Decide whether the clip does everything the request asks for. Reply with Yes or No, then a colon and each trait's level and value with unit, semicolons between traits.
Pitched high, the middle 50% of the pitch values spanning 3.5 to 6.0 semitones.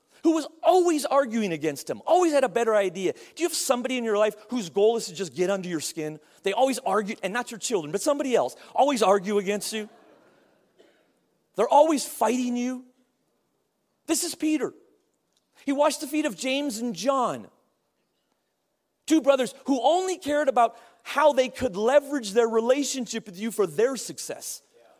Yes: very high, 250 Hz; wide, 5.4 semitones